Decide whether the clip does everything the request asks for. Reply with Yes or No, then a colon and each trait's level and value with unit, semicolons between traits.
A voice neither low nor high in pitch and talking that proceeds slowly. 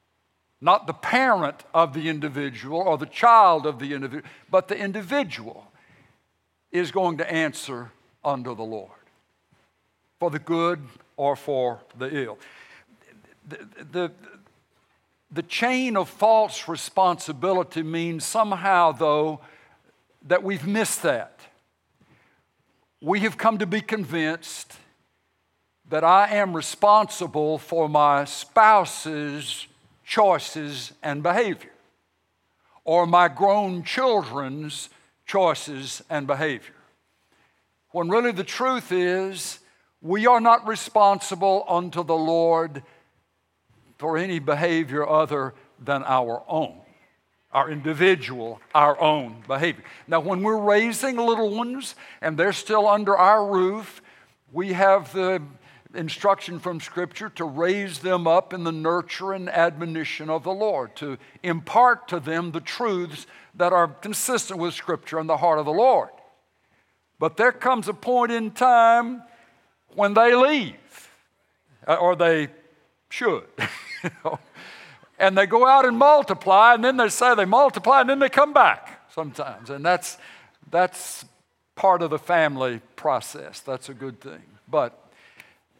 Yes: medium, 170 Hz; slow, 125 wpm